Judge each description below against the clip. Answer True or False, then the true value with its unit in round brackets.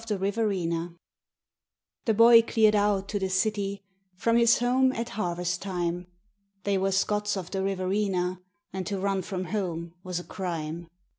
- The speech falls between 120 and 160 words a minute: True (155 wpm)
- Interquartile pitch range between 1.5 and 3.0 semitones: True (2.7 semitones)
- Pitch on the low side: False (195 Hz)